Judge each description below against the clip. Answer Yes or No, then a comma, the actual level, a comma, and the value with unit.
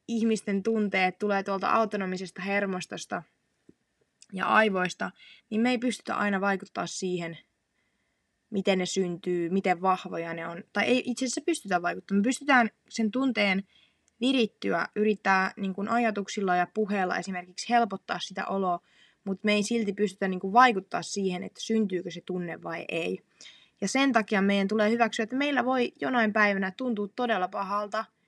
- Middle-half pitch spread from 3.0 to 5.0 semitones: Yes, average, 3.3 semitones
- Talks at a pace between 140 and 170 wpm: Yes, average, 150 wpm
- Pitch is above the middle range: Yes, high, 200 Hz